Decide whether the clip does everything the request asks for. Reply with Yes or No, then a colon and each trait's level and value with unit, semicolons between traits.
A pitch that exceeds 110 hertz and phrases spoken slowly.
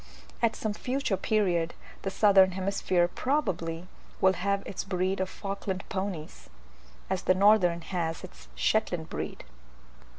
Yes: high, 190 Hz; slow, 130 wpm